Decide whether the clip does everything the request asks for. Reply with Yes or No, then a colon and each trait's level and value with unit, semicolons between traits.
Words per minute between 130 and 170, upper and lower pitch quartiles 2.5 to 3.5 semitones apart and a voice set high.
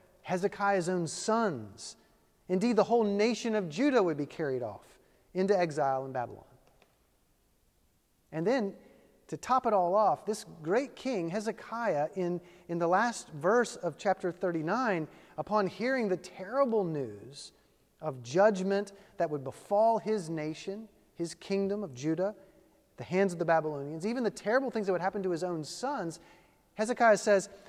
No: average, 150 wpm; average, 4.1 semitones; high, 195 Hz